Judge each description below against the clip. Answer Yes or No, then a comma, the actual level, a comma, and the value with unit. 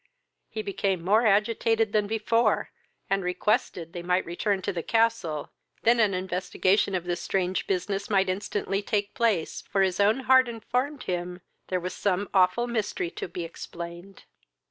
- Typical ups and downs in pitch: Yes, average, 3.5 semitones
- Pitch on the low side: No, high, 195 Hz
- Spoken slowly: No, average, 160 wpm